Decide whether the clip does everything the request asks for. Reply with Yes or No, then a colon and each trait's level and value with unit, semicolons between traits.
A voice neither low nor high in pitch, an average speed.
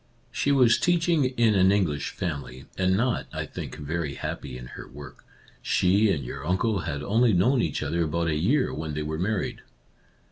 No: very low, 90 Hz; average, 185 wpm